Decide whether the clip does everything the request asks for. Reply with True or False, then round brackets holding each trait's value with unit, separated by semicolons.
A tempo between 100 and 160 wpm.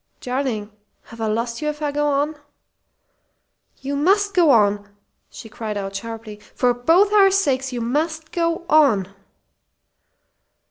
True (140 wpm)